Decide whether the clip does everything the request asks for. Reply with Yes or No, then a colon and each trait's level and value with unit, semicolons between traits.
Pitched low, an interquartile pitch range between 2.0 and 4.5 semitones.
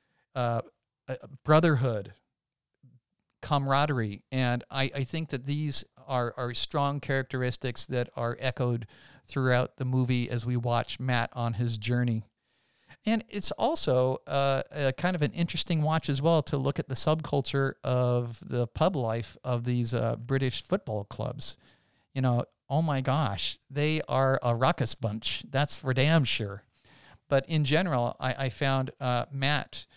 Yes: low, 130 Hz; average, 2.8 semitones